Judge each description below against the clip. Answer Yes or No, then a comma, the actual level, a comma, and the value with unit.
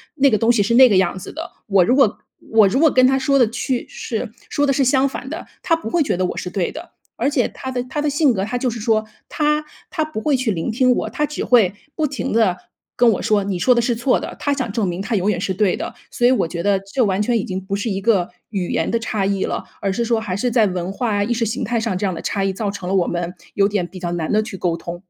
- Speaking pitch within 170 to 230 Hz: Yes, high, 220 Hz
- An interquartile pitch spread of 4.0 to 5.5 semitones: Yes, average, 4.9 semitones